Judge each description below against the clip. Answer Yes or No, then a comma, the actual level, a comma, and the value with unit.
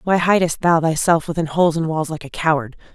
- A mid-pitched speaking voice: Yes, medium, 160 Hz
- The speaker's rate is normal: No, fast, 225 wpm